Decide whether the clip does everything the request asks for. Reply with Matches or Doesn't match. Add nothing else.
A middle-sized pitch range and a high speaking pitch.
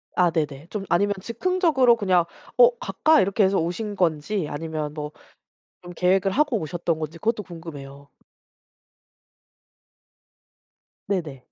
Doesn't match